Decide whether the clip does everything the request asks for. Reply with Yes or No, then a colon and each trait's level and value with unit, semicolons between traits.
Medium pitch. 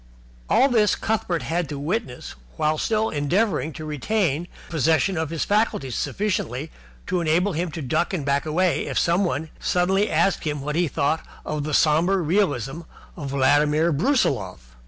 Yes: medium, 160 Hz